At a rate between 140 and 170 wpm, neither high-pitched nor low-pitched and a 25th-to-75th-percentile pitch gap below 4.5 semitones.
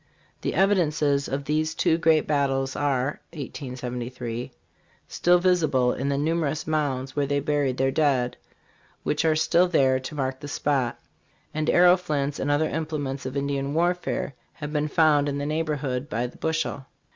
Yes: average, 160 wpm; medium, 145 Hz; average, 2.7 semitones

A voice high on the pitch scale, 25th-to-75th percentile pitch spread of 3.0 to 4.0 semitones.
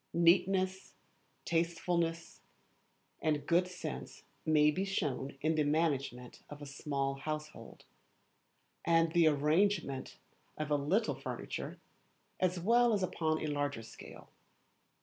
No: medium, 155 Hz; average, 3.5 semitones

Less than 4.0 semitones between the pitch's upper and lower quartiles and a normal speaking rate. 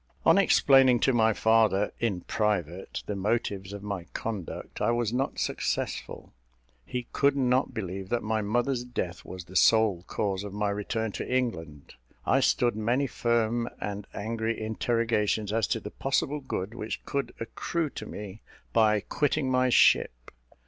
Yes: average, 3.2 semitones; average, 155 wpm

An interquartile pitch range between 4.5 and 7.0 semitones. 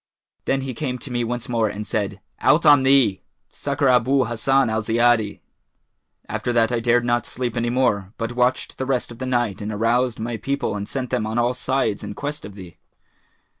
No: narrow, 2.6 semitones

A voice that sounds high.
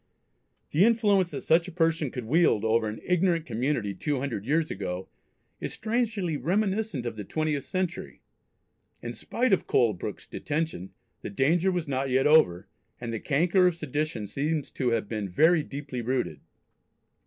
No: medium, 150 Hz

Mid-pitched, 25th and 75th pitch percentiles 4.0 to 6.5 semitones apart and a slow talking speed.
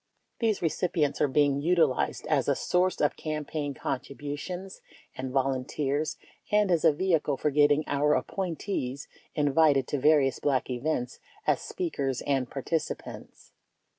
No: medium, 145 Hz; average, 3.1 semitones; slow, 130 wpm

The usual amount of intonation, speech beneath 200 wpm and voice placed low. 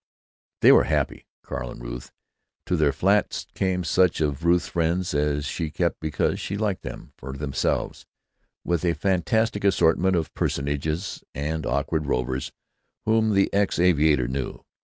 Yes: average, 4.5 semitones; average, 150 wpm; very low, 80 Hz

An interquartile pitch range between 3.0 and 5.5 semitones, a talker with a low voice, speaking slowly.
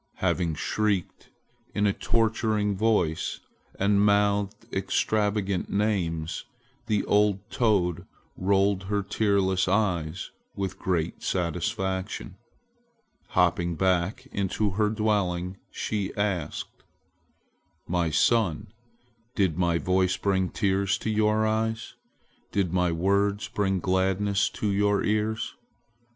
No: narrow, 2.4 semitones; low, 100 Hz; slow, 105 wpm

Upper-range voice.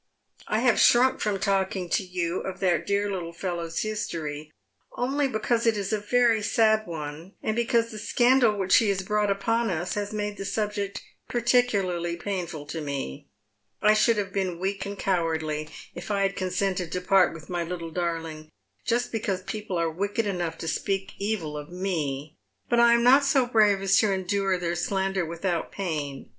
Yes: high, 195 Hz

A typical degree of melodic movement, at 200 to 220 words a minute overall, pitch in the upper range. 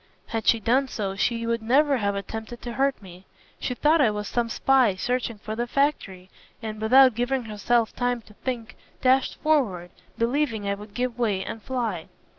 No: average, 3.4 semitones; average, 185 wpm; high, 230 Hz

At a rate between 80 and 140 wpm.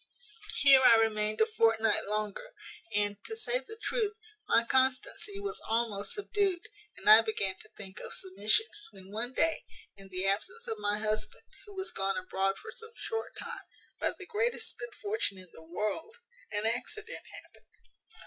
No: average, 170 wpm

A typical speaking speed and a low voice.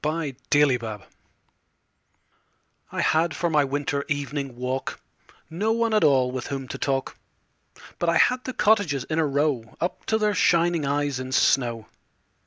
No: average, 155 wpm; medium, 145 Hz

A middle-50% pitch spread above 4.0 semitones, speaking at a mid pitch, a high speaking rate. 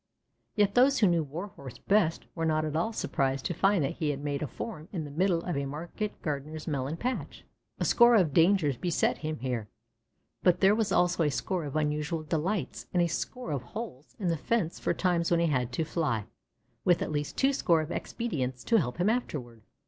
Yes: average, 4.8 semitones; medium, 165 Hz; fast, 210 wpm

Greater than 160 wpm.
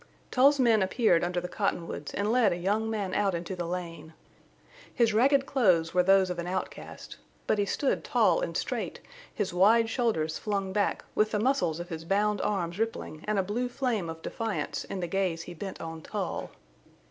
Yes: average, 195 wpm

